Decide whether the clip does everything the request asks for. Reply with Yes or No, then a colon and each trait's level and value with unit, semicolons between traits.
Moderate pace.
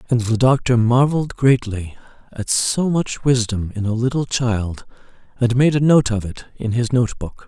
Yes: average, 185 wpm